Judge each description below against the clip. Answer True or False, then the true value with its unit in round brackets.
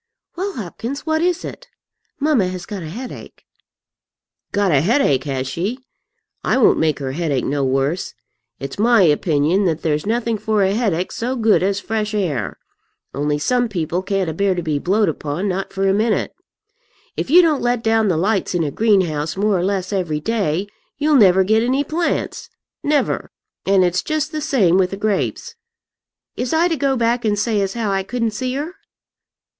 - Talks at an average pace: True (185 wpm)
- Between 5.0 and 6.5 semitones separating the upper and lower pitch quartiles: True (5.6 semitones)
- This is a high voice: True (200 Hz)